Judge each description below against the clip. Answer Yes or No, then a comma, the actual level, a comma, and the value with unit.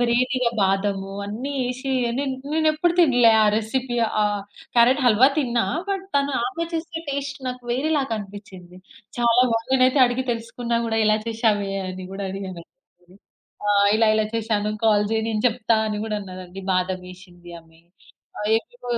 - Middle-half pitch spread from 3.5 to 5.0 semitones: Yes, average, 4.1 semitones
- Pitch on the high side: Yes, high, 225 Hz